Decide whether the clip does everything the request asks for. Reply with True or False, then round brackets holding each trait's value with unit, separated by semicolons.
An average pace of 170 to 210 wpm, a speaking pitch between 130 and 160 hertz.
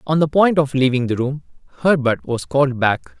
True (205 wpm; 140 Hz)